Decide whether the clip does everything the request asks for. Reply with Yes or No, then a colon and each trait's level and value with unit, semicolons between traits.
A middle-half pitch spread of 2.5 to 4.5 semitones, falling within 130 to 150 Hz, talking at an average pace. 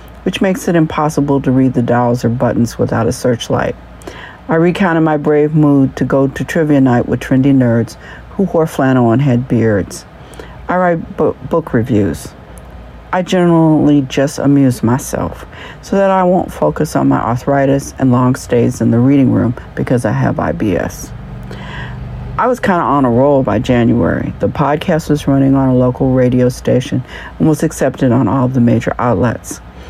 Yes: average, 4.2 semitones; low, 135 Hz; average, 175 wpm